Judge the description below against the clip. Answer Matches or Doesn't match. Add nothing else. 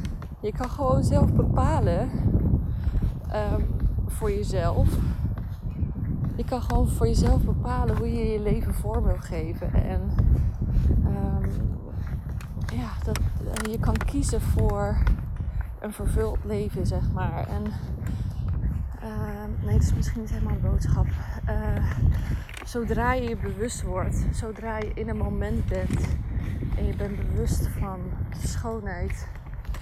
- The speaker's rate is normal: Doesn't match